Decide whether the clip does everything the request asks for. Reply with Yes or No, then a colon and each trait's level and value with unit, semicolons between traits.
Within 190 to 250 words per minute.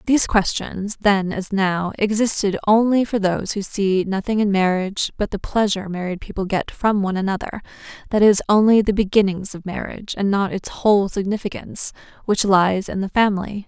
No: average, 175 wpm